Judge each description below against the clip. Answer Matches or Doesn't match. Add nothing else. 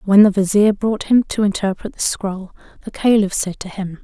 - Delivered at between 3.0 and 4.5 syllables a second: Doesn't match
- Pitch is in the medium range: Doesn't match